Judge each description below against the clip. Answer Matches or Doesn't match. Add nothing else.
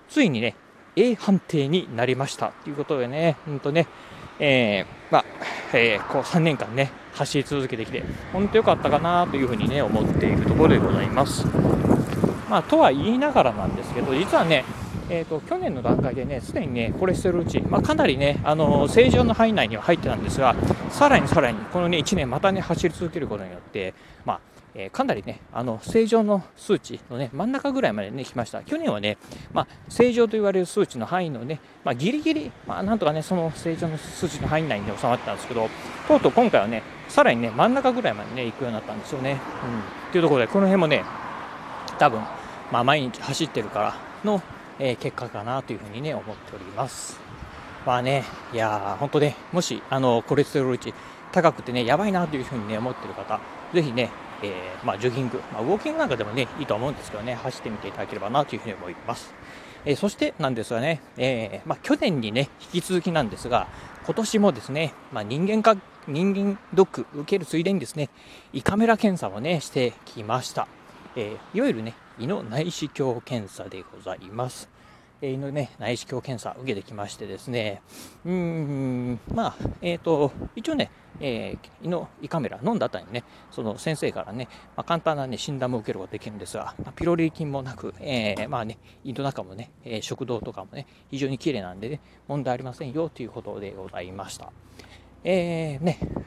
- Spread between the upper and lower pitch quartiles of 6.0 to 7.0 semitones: Matches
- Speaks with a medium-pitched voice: Matches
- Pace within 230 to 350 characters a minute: Doesn't match